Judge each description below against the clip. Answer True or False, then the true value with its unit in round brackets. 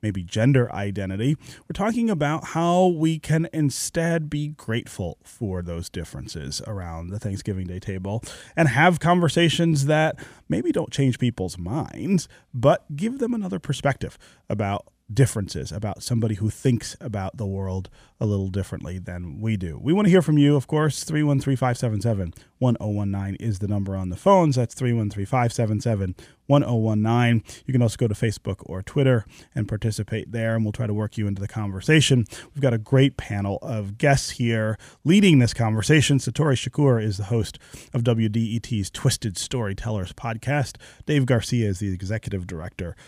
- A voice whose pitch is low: True (115 Hz)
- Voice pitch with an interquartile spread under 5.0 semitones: False (5.6 semitones)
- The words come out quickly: False (160 wpm)